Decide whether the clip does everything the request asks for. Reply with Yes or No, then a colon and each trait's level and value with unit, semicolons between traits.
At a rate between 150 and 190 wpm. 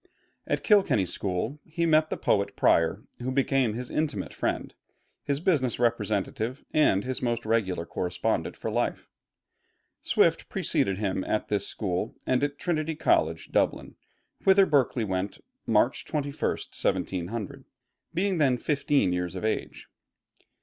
No: slow, 135 wpm